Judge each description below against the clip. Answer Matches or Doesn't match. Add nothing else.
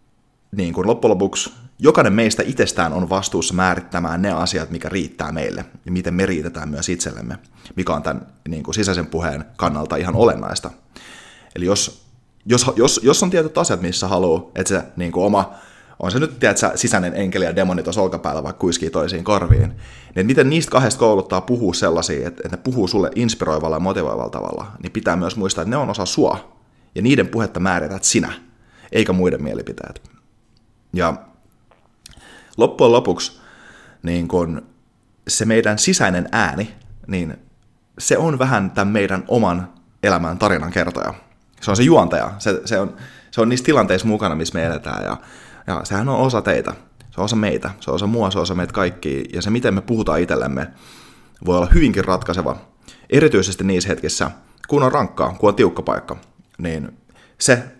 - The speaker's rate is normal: Doesn't match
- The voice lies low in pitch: Matches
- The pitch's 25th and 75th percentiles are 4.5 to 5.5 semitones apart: Doesn't match